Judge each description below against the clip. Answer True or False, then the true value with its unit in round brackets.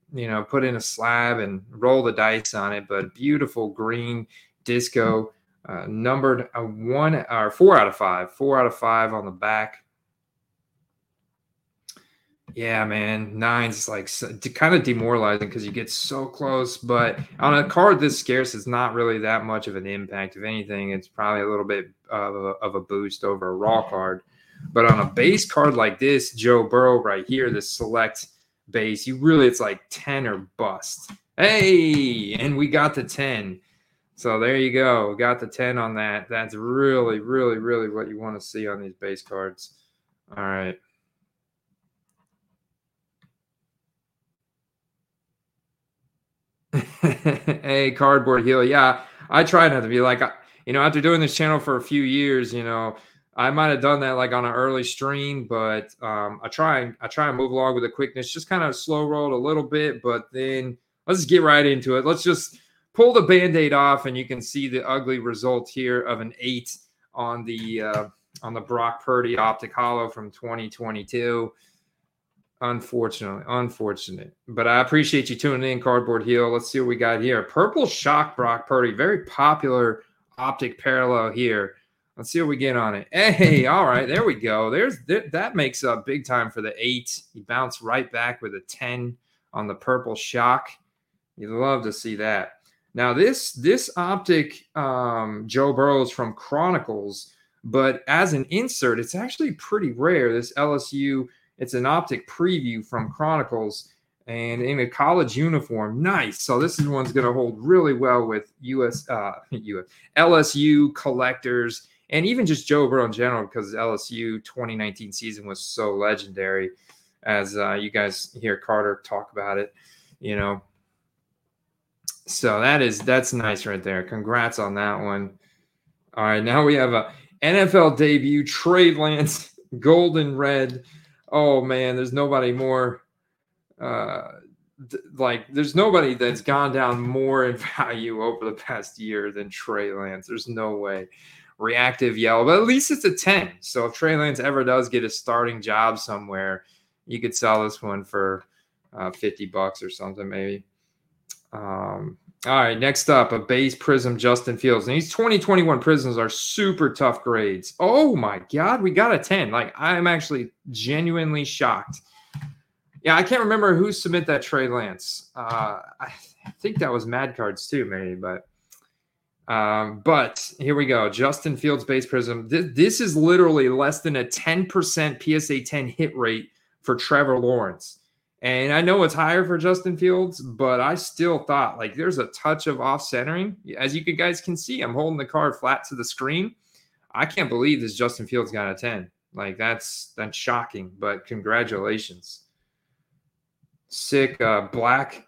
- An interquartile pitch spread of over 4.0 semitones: True (4.9 semitones)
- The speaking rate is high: False (170 wpm)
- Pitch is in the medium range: False (130 Hz)